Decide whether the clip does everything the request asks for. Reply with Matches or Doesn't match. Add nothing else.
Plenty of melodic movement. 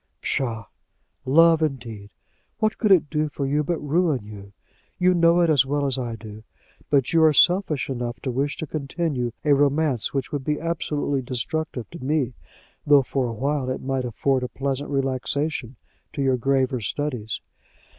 Doesn't match